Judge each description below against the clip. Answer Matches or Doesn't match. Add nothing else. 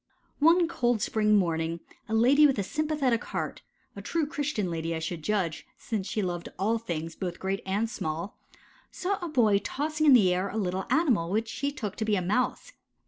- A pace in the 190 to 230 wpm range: Matches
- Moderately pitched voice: Doesn't match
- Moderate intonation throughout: Doesn't match